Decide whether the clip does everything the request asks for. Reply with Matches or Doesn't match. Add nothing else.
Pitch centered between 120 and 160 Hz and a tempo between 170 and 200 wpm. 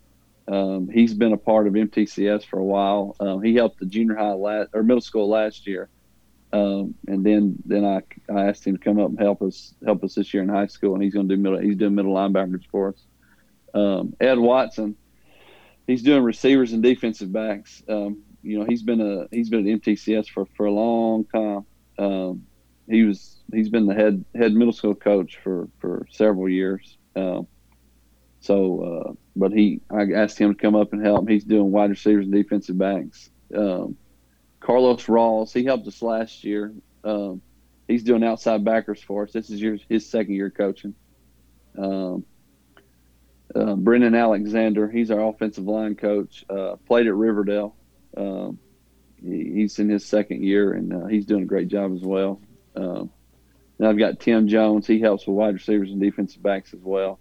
Doesn't match